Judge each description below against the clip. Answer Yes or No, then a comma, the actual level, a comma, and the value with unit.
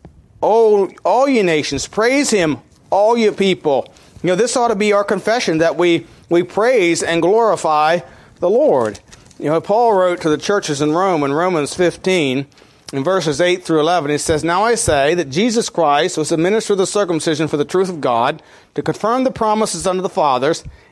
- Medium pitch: Yes, medium, 180 Hz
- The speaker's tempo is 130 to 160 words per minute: No, average, 195 wpm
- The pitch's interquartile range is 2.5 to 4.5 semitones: No, average, 5.3 semitones